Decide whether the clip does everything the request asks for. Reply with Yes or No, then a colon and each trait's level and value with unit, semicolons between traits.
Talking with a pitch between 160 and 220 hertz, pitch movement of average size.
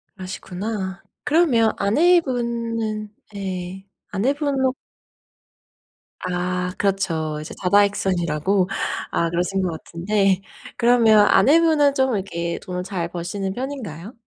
Yes: high, 200 Hz; average, 4.7 semitones